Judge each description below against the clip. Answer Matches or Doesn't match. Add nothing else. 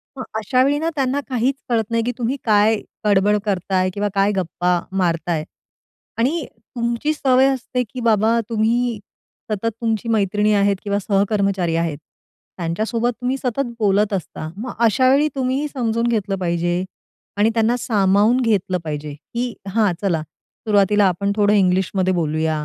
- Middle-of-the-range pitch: Doesn't match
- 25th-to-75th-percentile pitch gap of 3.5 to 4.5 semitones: Matches